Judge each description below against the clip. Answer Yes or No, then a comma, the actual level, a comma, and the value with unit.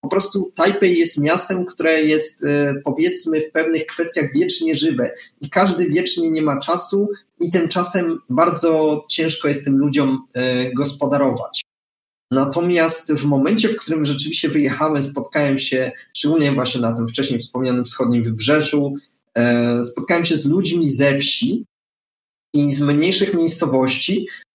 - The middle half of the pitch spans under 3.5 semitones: No, average, 3.8 semitones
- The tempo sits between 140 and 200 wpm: No, average, 130 wpm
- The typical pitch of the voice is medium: Yes, medium, 155 Hz